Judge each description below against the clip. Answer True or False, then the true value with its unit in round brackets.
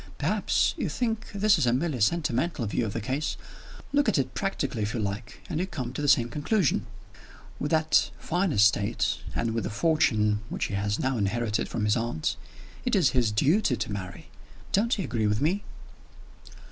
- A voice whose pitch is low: True (125 Hz)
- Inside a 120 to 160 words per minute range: False (185 wpm)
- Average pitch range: False (7.7 semitones)